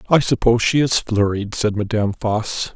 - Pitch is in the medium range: No, low, 110 Hz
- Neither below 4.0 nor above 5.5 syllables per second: Yes, 5.3 syllables/s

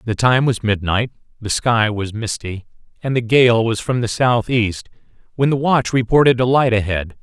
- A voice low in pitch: Yes, low, 115 Hz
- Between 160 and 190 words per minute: Yes, average, 185 wpm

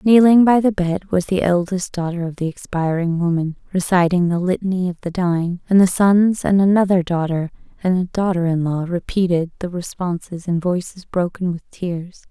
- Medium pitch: Yes, medium, 180 Hz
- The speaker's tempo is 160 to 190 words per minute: Yes, average, 180 wpm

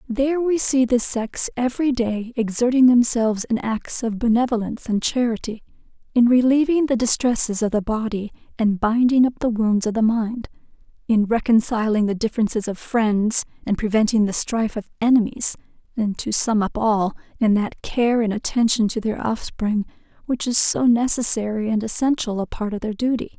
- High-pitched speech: Yes, high, 230 Hz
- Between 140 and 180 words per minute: Yes, average, 170 wpm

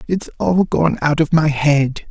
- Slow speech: No, average, 200 wpm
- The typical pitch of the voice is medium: Yes, medium, 155 Hz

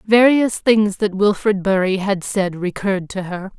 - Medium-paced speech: Yes, average, 165 wpm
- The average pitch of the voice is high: Yes, high, 200 Hz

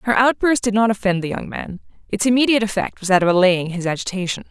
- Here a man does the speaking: No, female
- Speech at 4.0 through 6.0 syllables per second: No, 6.6 syllables/s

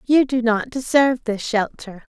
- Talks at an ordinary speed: Yes, average, 165 wpm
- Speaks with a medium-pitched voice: No, high, 240 Hz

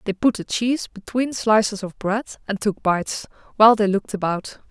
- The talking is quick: No, average, 190 wpm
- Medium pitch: No, high, 210 Hz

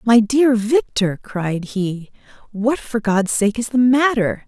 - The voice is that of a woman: Yes, female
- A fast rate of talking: No, average, 160 wpm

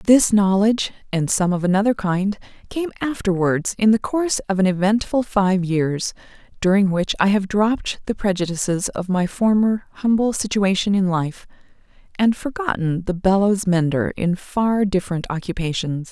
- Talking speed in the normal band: Yes, average, 150 wpm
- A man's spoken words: No, female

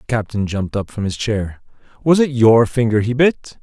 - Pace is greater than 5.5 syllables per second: No, 5.3 syllables/s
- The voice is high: No, low, 115 Hz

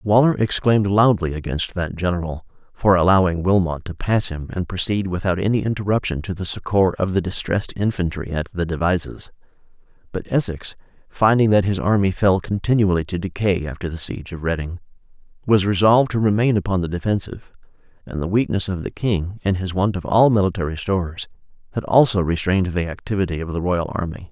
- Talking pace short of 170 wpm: No, average, 175 wpm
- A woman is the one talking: No, male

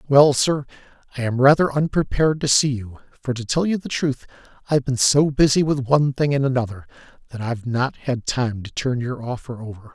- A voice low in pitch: Yes, low, 130 Hz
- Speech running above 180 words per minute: Yes, fast, 205 wpm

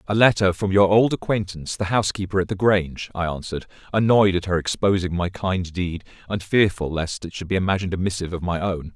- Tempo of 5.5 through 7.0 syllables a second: Yes, 6.2 syllables/s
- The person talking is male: Yes, male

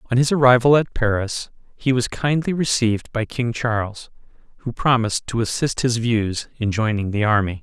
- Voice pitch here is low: Yes, low, 115 Hz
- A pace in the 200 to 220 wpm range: No, average, 175 wpm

